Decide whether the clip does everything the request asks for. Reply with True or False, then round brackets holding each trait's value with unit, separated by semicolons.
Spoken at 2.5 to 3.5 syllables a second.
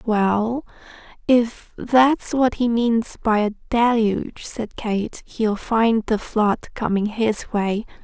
True (3.1 syllables/s)